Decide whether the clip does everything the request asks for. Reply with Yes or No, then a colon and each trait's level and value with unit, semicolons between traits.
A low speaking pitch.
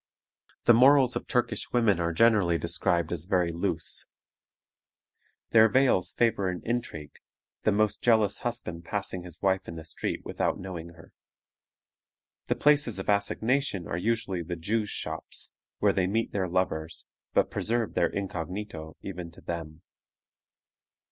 Yes: very low, 95 Hz